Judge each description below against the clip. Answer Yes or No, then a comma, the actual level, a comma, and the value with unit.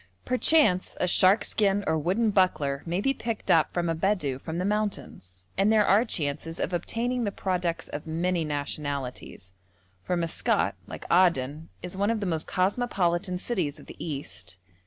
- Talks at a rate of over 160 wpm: Yes, average, 170 wpm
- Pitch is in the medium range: Yes, medium, 180 Hz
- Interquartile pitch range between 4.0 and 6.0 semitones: Yes, average, 4.8 semitones